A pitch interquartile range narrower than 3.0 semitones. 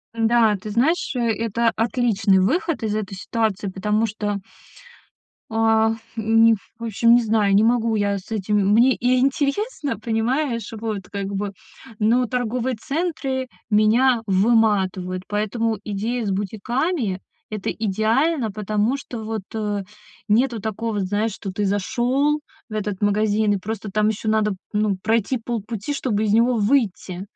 Yes: narrow, 2.5 semitones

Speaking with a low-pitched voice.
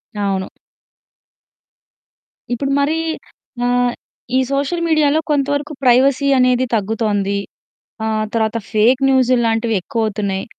No: high, 245 Hz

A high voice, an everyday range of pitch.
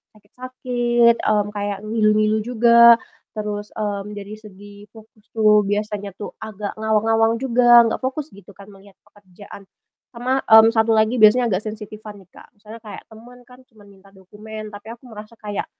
No: high, 215 Hz; narrow, 2.0 semitones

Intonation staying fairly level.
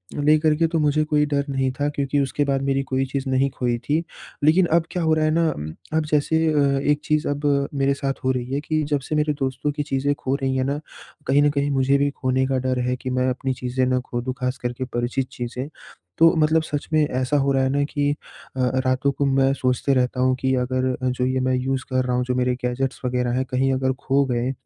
Yes: narrow, 2.1 semitones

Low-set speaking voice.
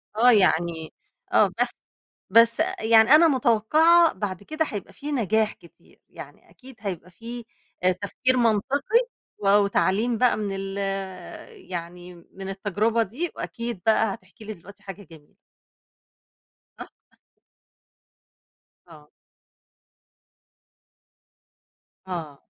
No: high, 210 Hz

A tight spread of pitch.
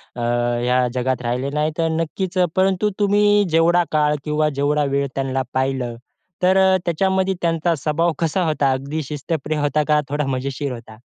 No: average, 4.0 semitones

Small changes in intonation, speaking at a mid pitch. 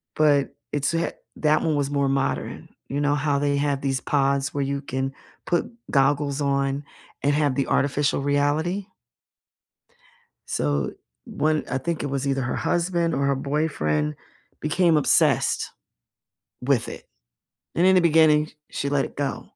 Yes: narrow, 1.9 semitones; medium, 145 Hz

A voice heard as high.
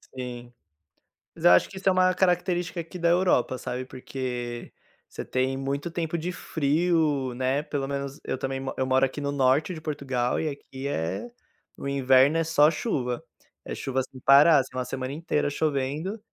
No: medium, 140 Hz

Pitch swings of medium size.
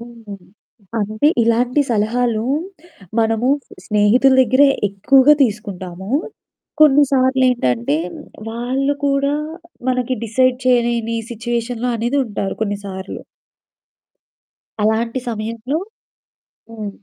Yes: average, 3.1 semitones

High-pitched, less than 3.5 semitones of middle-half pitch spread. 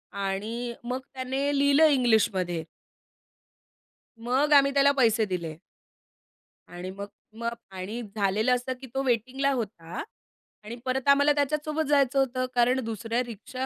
No: high, 245 Hz; average, 4.2 semitones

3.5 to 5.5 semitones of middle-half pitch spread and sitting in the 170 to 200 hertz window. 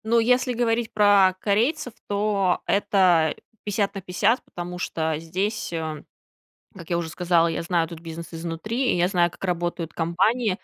Yes: average, 4.0 semitones; medium, 185 Hz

